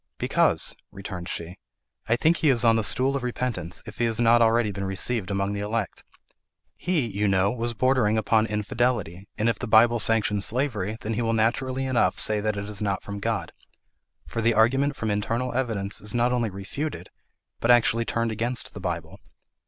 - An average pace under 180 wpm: No, average, 190 wpm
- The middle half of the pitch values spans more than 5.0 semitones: No, average, 2.9 semitones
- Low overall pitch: Yes, low, 115 Hz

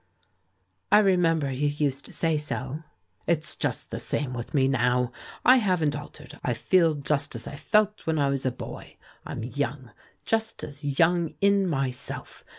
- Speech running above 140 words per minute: Yes, average, 170 wpm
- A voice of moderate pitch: Yes, medium, 145 Hz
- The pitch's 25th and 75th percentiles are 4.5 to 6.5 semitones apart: No, average, 4.1 semitones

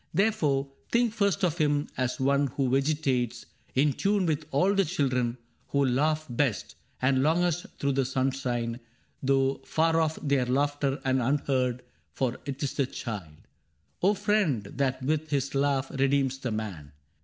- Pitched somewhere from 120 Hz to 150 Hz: Yes, medium, 140 Hz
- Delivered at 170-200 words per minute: No, average, 155 wpm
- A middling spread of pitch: Yes, average, 3.2 semitones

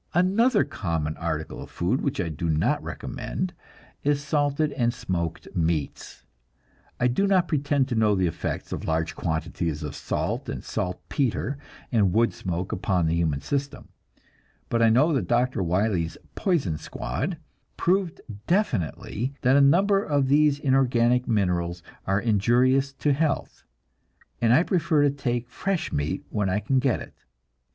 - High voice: No, low, 120 Hz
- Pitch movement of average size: No, wide, 8.1 semitones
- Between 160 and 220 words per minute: No, average, 150 wpm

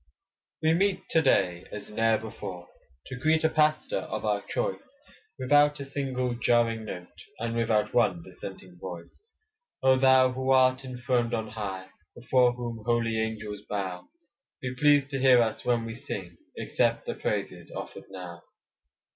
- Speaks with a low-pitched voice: Yes, low, 120 Hz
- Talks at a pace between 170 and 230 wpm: No, average, 155 wpm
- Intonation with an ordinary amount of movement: Yes, average, 4.0 semitones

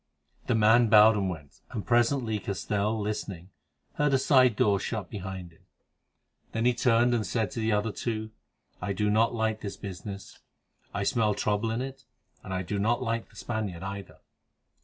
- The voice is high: No, low, 110 Hz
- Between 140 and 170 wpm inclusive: No, average, 180 wpm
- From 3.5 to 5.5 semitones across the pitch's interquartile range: No, average, 2.7 semitones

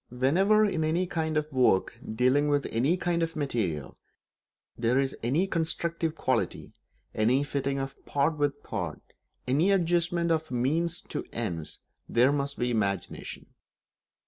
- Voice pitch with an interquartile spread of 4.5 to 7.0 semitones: Yes, average, 4.8 semitones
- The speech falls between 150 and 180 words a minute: No, average, 140 wpm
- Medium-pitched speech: Yes, medium, 145 Hz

